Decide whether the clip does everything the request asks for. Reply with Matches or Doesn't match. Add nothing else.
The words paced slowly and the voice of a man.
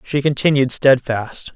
Matches